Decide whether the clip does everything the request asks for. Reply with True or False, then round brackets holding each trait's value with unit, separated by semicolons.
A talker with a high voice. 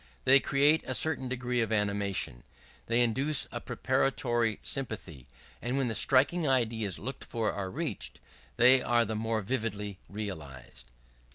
False (115 Hz)